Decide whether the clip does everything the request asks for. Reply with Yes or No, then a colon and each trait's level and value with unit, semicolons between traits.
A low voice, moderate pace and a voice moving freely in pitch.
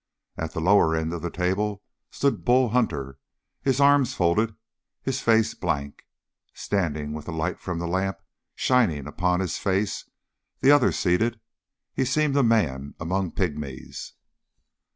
Yes: very low, 95 Hz; average, 145 wpm; wide, 6.4 semitones